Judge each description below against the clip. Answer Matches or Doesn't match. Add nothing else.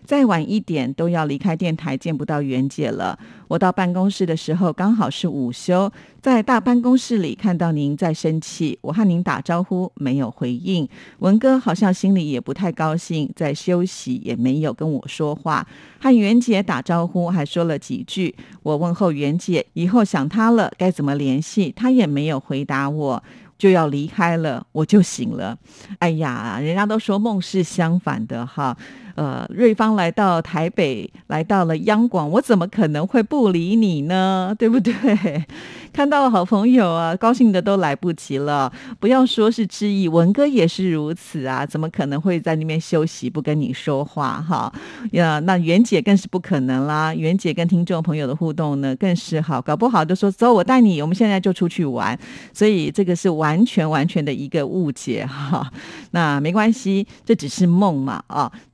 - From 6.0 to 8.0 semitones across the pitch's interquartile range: Doesn't match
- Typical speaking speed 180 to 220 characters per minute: Doesn't match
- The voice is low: Doesn't match